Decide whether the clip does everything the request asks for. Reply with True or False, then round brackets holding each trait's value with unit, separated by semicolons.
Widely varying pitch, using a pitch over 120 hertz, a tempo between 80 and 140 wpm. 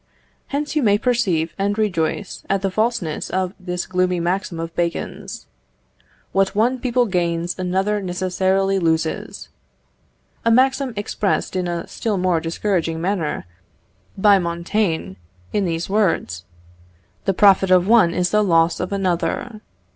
False (3.3 semitones; 185 Hz; 135 wpm)